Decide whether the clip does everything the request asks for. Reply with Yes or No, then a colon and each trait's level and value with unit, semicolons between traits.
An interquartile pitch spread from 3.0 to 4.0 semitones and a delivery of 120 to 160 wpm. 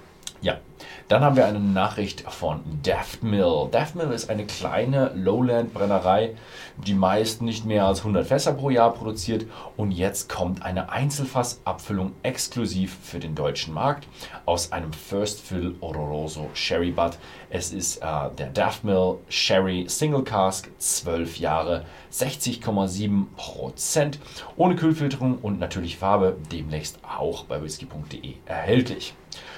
No: average, 4.6 semitones; average, 130 wpm